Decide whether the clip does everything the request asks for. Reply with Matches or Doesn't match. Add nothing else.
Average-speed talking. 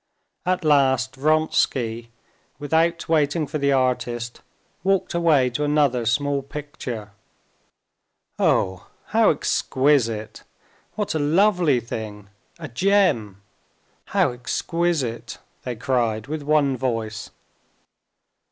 Doesn't match